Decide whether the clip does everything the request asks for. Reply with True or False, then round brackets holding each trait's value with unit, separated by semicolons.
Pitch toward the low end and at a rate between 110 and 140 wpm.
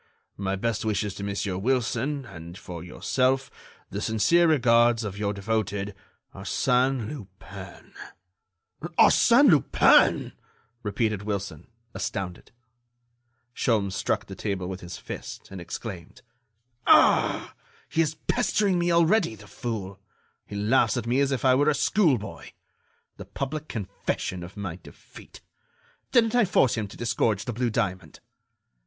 True (110 Hz; 135 wpm)